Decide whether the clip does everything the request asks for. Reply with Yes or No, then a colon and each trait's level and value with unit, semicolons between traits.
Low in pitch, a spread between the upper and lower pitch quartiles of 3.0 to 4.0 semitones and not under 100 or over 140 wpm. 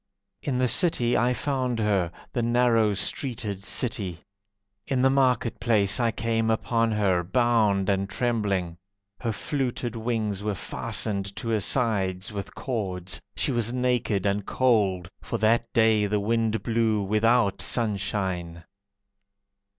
Yes: low, 110 Hz; average, 3.3 semitones; slow, 135 wpm